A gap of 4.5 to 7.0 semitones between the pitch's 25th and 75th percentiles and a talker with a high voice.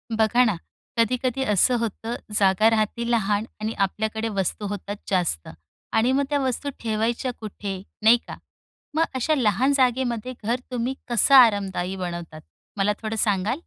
No: average, 3.3 semitones; high, 220 Hz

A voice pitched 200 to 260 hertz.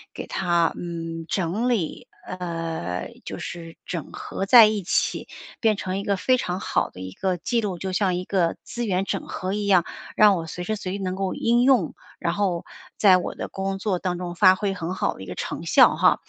No: medium, 185 Hz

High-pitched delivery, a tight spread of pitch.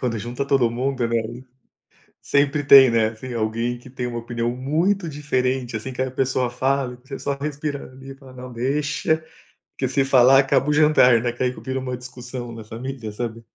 No: low, 130 Hz; narrow, 2.3 semitones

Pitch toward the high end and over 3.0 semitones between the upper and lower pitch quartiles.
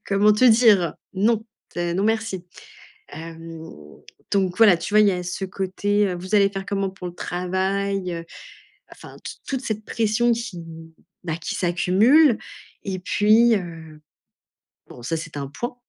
Yes: high, 195 Hz; average, 3.5 semitones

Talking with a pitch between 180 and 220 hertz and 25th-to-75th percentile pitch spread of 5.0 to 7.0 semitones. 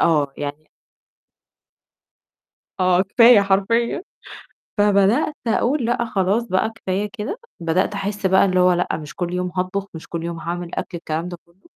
No: high, 190 Hz; average, 3.3 semitones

